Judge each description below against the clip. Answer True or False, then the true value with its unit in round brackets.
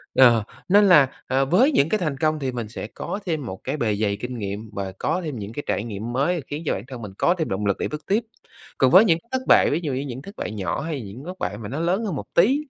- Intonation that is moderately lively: False (7.4 semitones)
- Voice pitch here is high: False (135 Hz)